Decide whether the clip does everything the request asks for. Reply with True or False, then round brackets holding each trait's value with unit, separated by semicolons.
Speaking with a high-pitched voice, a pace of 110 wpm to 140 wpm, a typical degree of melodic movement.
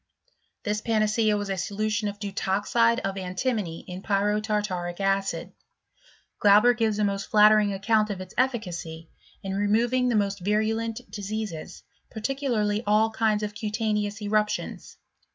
False (210 Hz; 135 wpm; 1.8 semitones)